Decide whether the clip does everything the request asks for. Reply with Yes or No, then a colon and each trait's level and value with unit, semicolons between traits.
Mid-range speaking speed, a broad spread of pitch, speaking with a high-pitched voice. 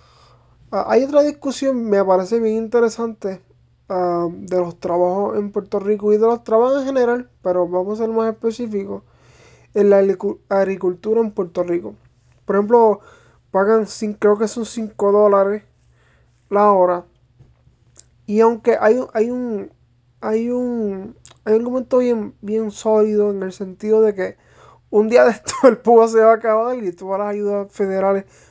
No: average, 155 wpm; average, 3.0 semitones; high, 210 Hz